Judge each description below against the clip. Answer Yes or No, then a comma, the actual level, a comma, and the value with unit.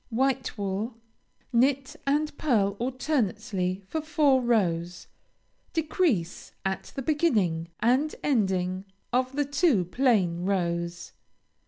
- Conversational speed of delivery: No, slow, 105 wpm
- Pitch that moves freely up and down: Yes, wide, 6.9 semitones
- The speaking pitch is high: Yes, high, 230 Hz